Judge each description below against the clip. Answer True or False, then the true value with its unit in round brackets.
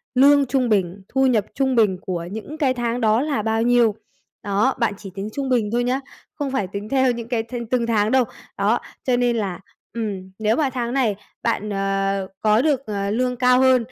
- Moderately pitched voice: False (235 Hz)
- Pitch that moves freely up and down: False (3.7 semitones)